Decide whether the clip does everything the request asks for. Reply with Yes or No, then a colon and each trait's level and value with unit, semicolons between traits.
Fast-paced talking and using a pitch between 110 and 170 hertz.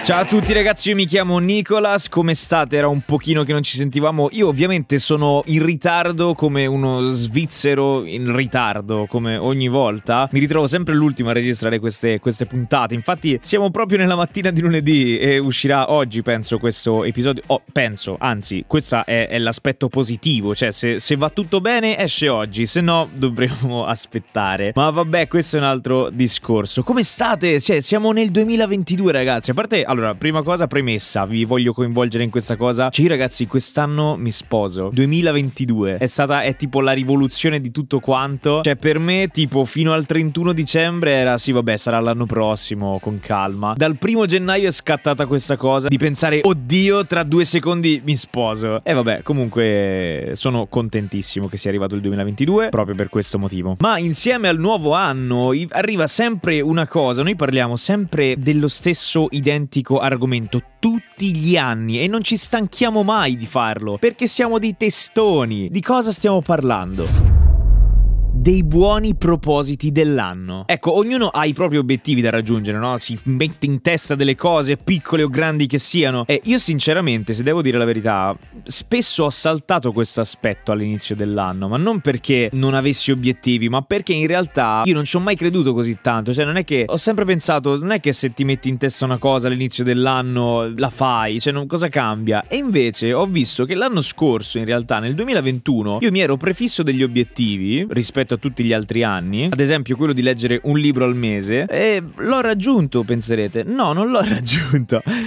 Yes: fast, 180 wpm; medium, 140 Hz